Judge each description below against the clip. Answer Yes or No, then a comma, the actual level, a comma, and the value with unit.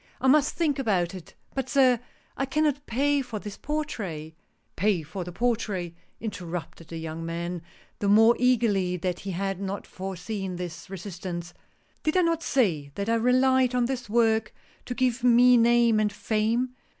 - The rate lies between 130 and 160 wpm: No, average, 185 wpm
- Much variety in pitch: Yes, wide, 5.7 semitones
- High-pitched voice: Yes, high, 215 Hz